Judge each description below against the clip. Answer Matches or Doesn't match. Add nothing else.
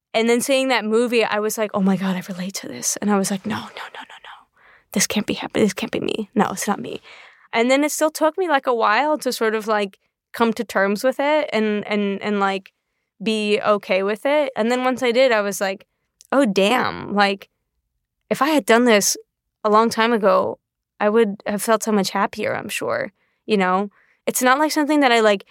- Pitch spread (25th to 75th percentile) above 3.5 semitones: Matches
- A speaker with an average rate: Doesn't match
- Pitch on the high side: Matches